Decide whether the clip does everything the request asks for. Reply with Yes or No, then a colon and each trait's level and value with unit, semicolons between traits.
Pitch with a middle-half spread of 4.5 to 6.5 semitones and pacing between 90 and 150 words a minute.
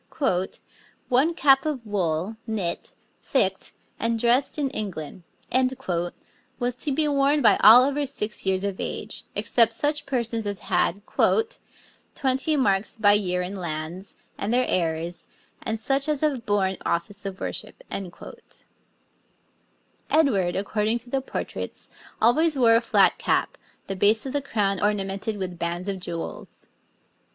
Yes: wide, 5.6 semitones; average, 140 wpm